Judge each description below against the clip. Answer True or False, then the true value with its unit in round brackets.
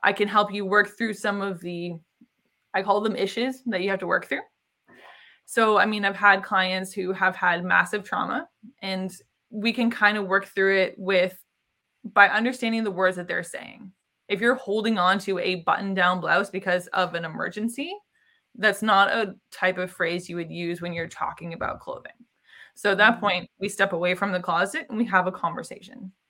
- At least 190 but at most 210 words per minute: True (200 wpm)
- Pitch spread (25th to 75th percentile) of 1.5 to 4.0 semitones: True (3.1 semitones)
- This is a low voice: False (200 Hz)